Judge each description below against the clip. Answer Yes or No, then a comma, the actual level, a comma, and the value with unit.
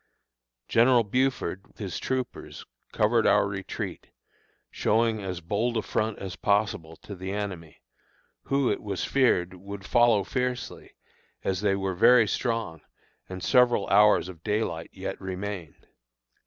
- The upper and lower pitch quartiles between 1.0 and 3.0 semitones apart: No, average, 3.7 semitones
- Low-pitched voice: Yes, low, 100 Hz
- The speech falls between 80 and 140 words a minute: Yes, slow, 135 wpm